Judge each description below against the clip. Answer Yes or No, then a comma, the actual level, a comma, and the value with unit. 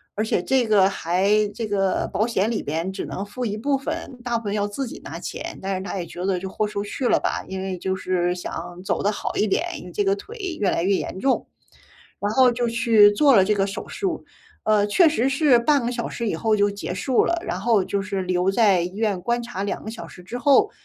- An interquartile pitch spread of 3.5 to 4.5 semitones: Yes, average, 4.0 semitones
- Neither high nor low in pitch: No, high, 210 Hz